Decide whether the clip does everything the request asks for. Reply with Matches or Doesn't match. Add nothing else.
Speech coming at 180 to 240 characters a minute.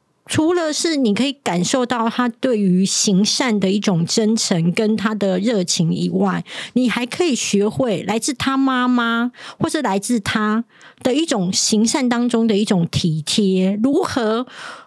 Matches